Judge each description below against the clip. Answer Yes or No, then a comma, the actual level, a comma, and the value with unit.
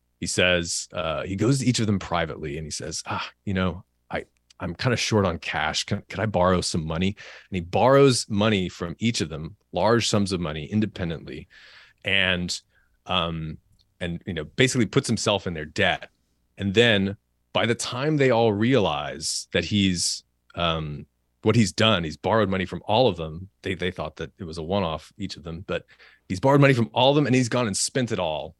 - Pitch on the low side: Yes, very low, 95 Hz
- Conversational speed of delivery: No, fast, 210 wpm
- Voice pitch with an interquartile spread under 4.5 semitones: No, average, 5.0 semitones